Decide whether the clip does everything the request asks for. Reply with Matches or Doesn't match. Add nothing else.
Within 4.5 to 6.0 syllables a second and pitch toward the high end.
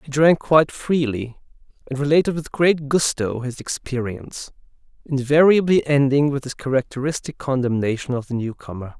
Doesn't match